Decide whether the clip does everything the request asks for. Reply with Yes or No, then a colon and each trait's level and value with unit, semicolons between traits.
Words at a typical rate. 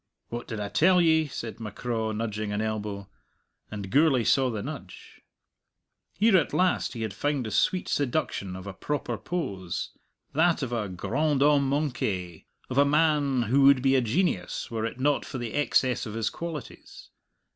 Yes: average, 175 wpm